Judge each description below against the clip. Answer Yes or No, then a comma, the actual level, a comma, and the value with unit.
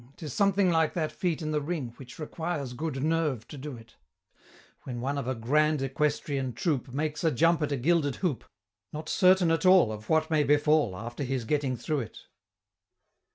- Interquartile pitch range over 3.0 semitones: Yes, average, 3.7 semitones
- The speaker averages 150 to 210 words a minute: Yes, average, 190 wpm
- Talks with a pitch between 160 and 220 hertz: No, medium, 150 Hz